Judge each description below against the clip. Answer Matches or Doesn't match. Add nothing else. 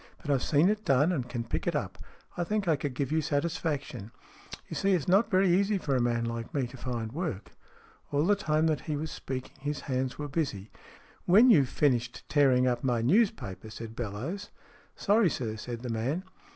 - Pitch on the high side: Doesn't match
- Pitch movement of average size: Doesn't match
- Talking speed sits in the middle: Doesn't match